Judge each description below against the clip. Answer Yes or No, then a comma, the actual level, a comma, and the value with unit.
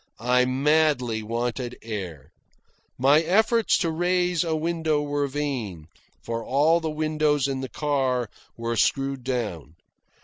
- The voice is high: No, medium, 140 Hz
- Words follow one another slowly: Yes, slow, 130 wpm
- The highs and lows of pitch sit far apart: No, average, 4.7 semitones